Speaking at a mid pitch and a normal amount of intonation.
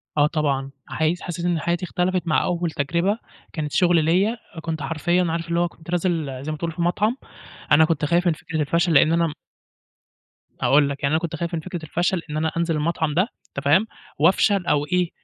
No: medium, 165 Hz; narrow, 2.3 semitones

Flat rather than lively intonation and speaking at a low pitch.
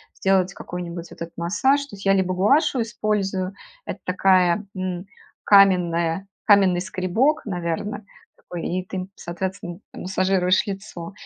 No: narrow, 2.1 semitones; medium, 185 Hz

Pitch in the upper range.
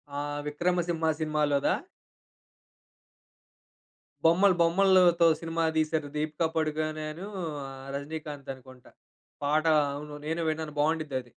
No: medium, 155 Hz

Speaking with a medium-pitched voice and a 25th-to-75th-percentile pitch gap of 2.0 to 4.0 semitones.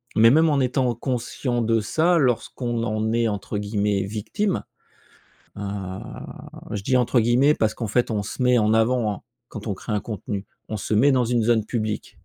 No: low, 115 Hz; average, 2.8 semitones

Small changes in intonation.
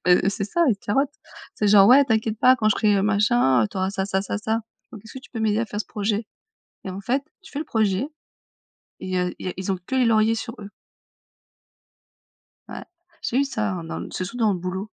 No: average, 3.2 semitones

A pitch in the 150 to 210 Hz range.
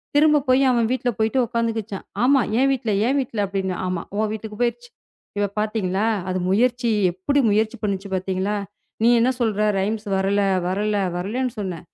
No: high, 220 Hz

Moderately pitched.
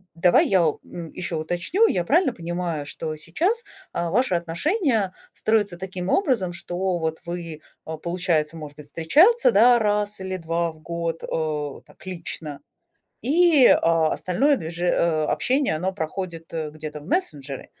Yes: medium, 175 Hz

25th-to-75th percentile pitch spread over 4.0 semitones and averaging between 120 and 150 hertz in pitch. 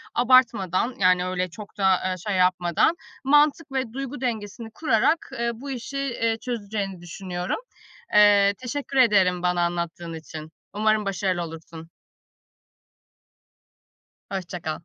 No: average, 5.2 semitones; high, 205 Hz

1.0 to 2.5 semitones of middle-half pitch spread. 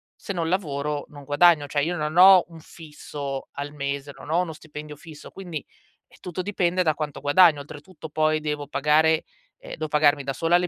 No: average, 2.9 semitones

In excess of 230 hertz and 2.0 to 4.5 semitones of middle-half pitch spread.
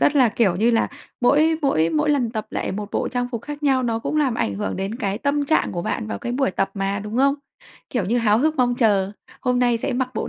No: high, 240 Hz; average, 5.1 semitones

